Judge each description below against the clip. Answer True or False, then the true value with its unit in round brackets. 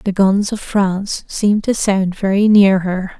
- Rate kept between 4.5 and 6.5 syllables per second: False (4.2 syllables/s)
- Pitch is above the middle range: True (195 Hz)